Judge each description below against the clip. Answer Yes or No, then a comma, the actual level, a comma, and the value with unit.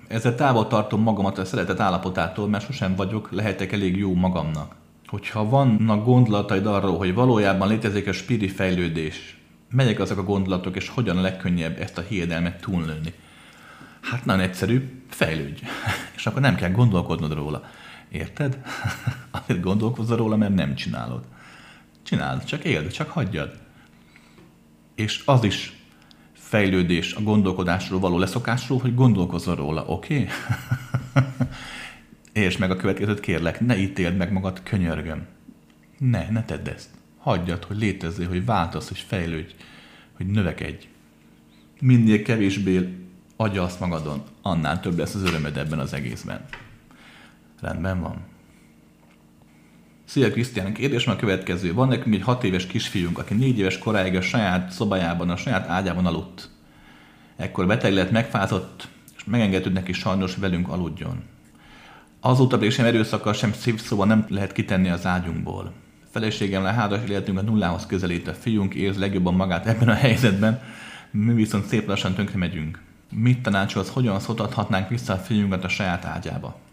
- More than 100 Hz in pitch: No, very low, 95 Hz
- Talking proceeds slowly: No, average, 145 wpm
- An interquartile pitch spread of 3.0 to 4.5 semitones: Yes, average, 4.0 semitones